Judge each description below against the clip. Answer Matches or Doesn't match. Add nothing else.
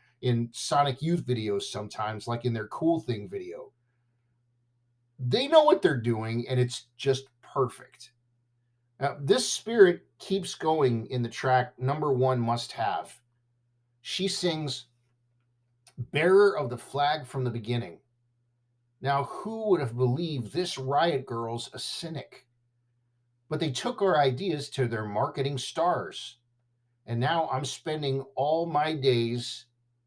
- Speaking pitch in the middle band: Doesn't match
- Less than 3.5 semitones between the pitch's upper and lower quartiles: Matches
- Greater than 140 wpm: Doesn't match